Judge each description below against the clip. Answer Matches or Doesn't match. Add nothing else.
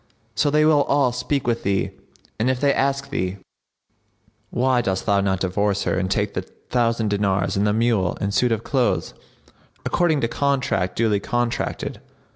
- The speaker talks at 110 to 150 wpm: Doesn't match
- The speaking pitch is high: Doesn't match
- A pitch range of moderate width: Matches